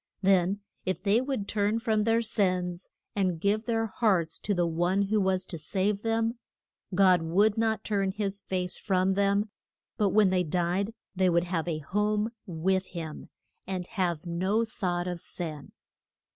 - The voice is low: No, high, 190 Hz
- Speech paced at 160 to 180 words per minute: Yes, average, 165 wpm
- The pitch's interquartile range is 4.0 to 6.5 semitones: No, average, 2.9 semitones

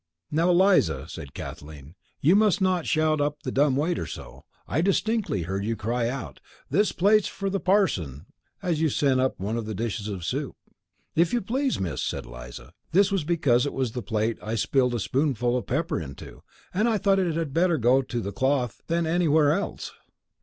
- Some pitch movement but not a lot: No, wide, 7.9 semitones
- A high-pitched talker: No, medium, 140 Hz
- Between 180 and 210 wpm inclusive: Yes, average, 195 wpm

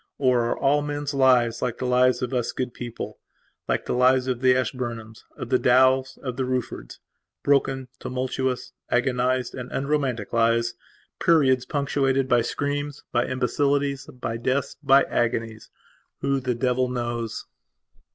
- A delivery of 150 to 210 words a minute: No, average, 140 wpm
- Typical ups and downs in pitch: No, narrow, 1.9 semitones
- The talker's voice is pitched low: Yes, low, 130 Hz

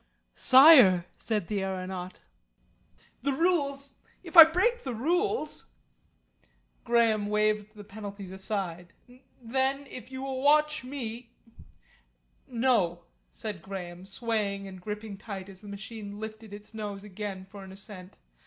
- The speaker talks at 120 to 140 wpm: Yes, slow, 135 wpm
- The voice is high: Yes, high, 210 Hz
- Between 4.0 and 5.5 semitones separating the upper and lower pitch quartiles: Yes, average, 5.2 semitones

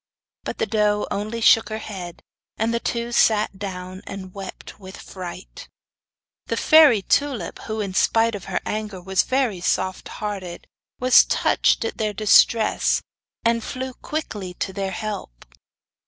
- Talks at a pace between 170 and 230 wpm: No, average, 150 wpm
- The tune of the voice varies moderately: Yes, average, 3.3 semitones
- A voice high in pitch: Yes, high, 210 Hz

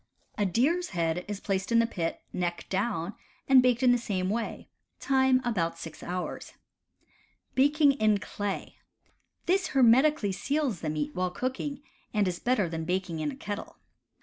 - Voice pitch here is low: No, high, 210 Hz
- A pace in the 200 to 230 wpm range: No, average, 165 wpm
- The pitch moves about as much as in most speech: No, wide, 6.4 semitones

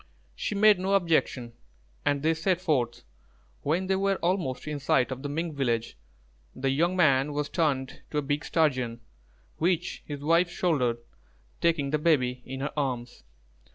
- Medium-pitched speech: Yes, medium, 150 Hz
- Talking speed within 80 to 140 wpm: No, average, 160 wpm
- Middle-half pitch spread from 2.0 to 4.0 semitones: No, average, 4.5 semitones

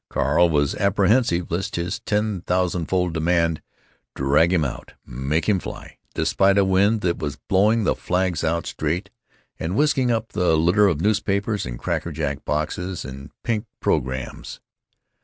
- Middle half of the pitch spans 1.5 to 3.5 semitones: No, average, 4.2 semitones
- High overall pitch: No, very low, 90 Hz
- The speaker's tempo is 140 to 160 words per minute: Yes, average, 150 wpm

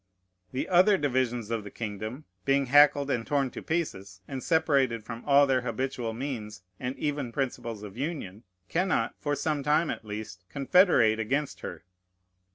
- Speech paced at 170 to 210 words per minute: No, average, 160 wpm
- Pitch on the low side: Yes, low, 130 Hz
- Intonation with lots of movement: No, average, 4.4 semitones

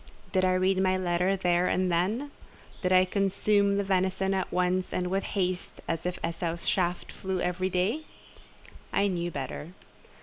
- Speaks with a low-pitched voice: No, medium, 185 Hz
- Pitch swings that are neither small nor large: No, narrow, 1.2 semitones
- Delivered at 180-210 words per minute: No, average, 165 wpm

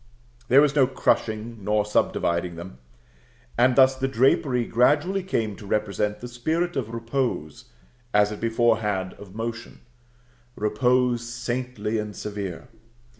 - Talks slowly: Yes, slow, 130 wpm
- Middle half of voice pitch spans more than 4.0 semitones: No, average, 3.5 semitones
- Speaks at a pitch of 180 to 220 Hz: No, low, 115 Hz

